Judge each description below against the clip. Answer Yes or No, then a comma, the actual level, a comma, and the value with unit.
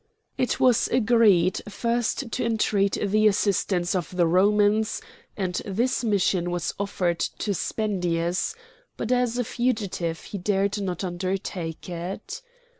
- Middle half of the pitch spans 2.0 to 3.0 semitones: No, average, 3.6 semitones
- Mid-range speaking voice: No, high, 200 Hz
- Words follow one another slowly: Yes, slow, 125 wpm